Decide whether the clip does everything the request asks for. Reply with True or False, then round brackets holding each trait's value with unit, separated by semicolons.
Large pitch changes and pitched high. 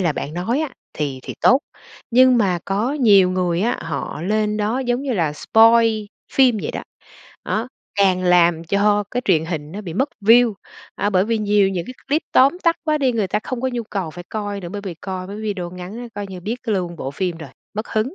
False (4.7 semitones; 205 Hz)